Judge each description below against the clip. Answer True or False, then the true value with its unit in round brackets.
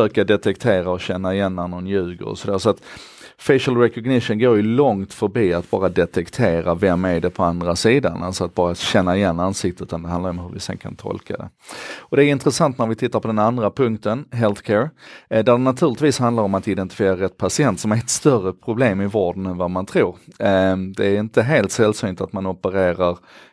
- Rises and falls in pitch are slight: False (3.8 semitones)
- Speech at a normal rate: False (205 wpm)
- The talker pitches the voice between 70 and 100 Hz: True (95 Hz)